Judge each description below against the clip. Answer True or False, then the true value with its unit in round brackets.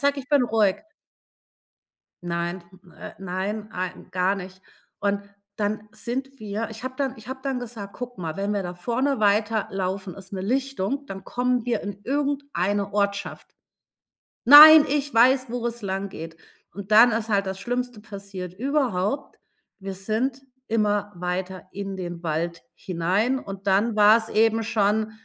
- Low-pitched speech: False (210 Hz)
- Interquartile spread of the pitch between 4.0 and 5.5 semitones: True (4.3 semitones)